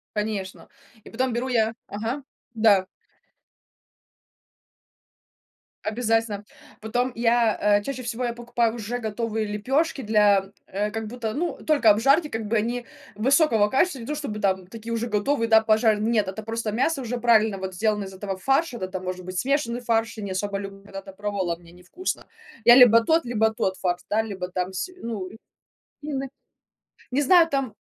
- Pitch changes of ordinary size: Yes, average, 3.1 semitones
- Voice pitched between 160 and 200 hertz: No, high, 220 Hz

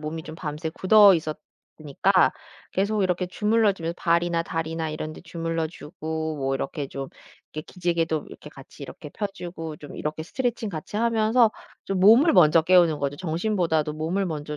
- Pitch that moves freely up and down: No, average, 3.7 semitones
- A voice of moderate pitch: Yes, medium, 165 Hz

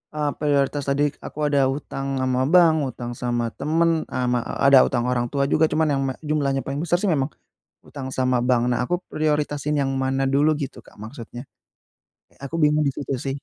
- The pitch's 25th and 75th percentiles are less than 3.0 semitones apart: Yes, narrow, 2.6 semitones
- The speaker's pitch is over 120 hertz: Yes, medium, 140 Hz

